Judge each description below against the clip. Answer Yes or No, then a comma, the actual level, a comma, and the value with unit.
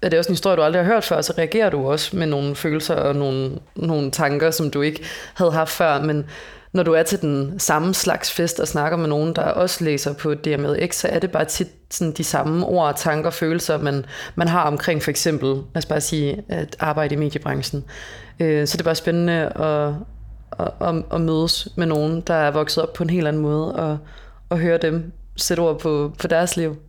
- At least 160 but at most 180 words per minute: No, average, 220 wpm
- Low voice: No, medium, 160 Hz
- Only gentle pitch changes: Yes, narrow, 2.2 semitones